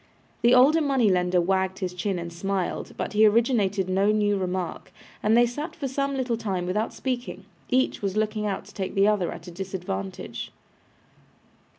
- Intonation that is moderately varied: Yes, average, 4.2 semitones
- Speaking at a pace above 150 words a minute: Yes, average, 180 wpm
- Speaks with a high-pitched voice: Yes, high, 205 Hz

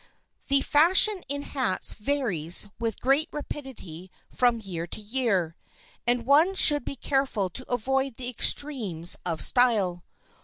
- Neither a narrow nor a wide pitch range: No, wide, 6.4 semitones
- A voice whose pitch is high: Yes, high, 245 Hz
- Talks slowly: Yes, slow, 130 wpm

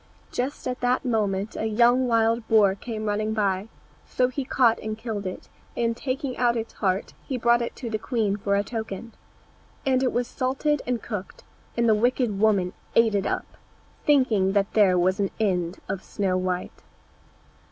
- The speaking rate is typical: Yes, average, 180 wpm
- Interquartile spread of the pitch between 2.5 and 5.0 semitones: Yes, average, 3.5 semitones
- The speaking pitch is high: Yes, high, 220 Hz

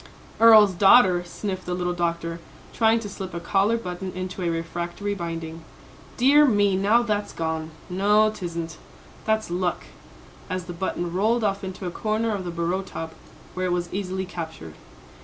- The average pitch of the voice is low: No, medium, 185 Hz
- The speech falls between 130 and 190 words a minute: Yes, average, 165 wpm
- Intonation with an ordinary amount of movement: Yes, average, 3.2 semitones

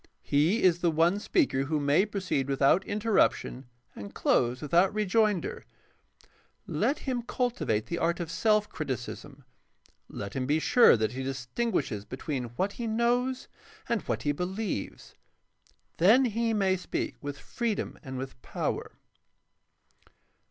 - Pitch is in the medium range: Yes, medium, 175 Hz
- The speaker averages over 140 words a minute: No, slow, 135 wpm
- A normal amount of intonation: No, wide, 8.2 semitones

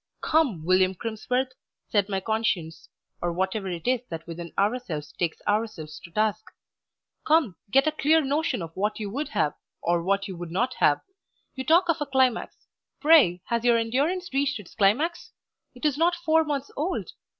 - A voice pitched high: Yes, high, 225 Hz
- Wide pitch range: Yes, wide, 7.6 semitones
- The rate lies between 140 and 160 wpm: No, average, 175 wpm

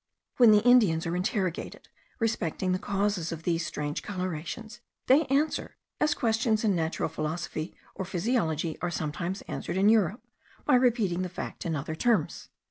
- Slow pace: No, average, 155 wpm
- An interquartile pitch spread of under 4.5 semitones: No, average, 5.3 semitones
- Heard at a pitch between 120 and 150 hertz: No, medium, 185 Hz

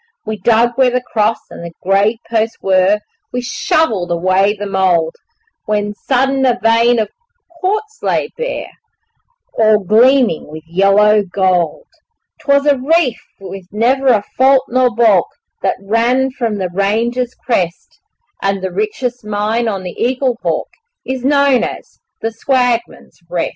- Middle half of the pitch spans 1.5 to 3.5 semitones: No, average, 4.4 semitones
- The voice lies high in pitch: Yes, high, 225 Hz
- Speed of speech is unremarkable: Yes, average, 145 wpm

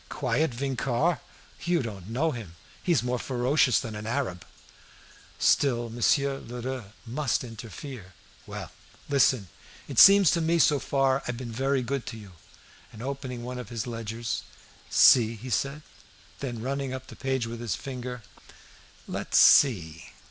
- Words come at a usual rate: Yes, average, 150 wpm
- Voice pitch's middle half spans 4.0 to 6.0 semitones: No, average, 3.2 semitones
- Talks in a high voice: No, low, 125 Hz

